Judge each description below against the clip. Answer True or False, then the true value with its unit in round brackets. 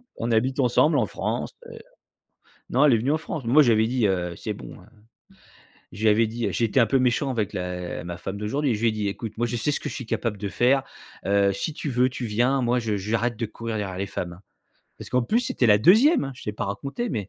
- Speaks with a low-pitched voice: True (115 Hz)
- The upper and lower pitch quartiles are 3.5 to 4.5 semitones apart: True (4.0 semitones)